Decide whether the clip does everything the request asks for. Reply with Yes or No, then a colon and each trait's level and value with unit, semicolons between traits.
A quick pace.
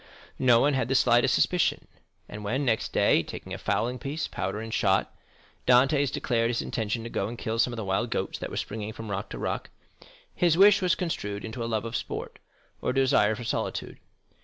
Yes: fast, 215 wpm